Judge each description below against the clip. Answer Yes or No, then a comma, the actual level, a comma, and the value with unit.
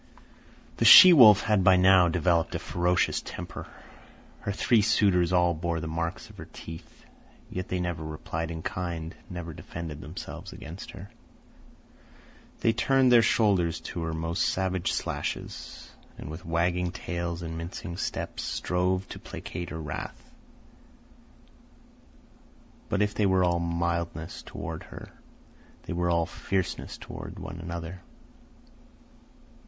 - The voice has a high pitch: No, very low, 85 Hz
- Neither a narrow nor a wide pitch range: No, narrow, 2.0 semitones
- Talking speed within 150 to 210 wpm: No, slow, 135 wpm